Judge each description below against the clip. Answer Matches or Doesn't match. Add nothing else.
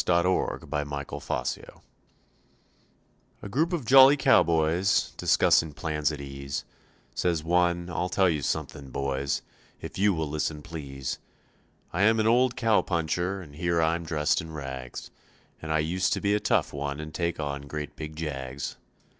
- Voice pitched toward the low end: Matches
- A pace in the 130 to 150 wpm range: Doesn't match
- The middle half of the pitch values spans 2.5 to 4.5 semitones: Matches